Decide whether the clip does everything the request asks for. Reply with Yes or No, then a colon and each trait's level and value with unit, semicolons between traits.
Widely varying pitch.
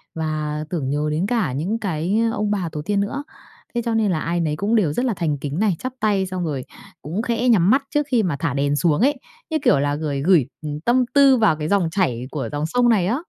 Yes: wide, 6.6 semitones